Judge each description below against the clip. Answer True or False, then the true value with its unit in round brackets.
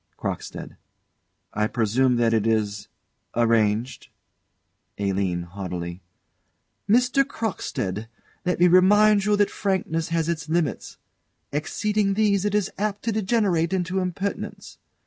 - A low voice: False (170 Hz)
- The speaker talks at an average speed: False (115 wpm)